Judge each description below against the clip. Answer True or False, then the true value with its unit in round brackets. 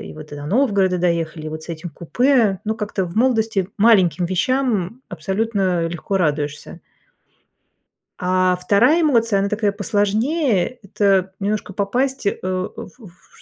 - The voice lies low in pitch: False (195 Hz)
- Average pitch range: True (4.0 semitones)